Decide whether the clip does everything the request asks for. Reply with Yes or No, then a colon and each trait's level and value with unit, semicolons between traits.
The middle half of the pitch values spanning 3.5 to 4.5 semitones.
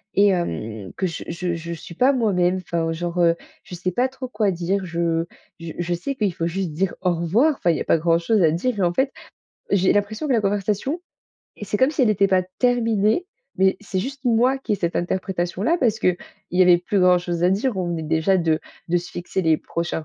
Yes: average, 4.0 semitones